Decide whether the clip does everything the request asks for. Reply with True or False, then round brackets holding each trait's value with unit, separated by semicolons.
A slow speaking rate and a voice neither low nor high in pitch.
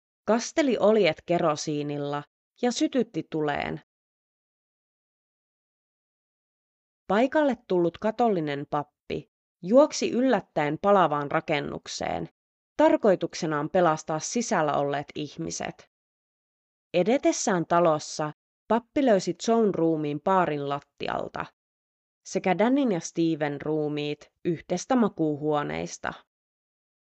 True (75 wpm; 170 Hz)